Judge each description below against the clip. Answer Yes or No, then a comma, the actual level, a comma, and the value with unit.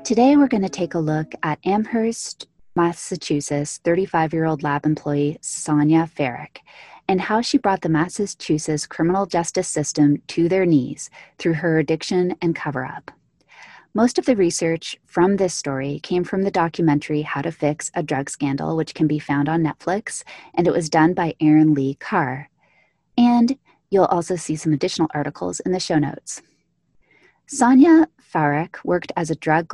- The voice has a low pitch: No, medium, 165 Hz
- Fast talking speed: No, average, 160 wpm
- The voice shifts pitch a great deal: No, average, 3.8 semitones